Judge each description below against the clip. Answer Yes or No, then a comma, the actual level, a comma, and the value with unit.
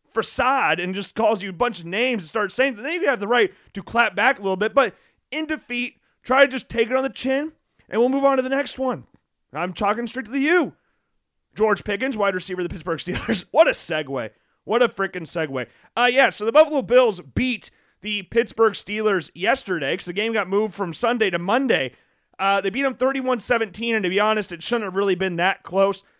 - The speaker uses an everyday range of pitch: Yes, average, 4.7 semitones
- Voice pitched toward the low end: No, high, 220 Hz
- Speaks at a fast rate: Yes, fast, 230 wpm